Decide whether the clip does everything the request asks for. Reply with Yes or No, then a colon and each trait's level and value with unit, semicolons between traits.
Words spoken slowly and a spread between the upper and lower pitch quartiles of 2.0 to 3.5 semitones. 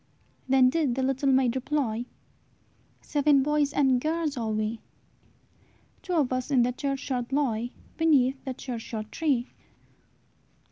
Yes: slow, 130 wpm; average, 2.9 semitones